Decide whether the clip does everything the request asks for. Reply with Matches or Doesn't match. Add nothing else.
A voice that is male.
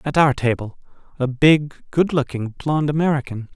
Matches